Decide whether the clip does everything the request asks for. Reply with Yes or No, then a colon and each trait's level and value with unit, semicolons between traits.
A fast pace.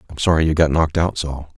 Yes: fast, 265 wpm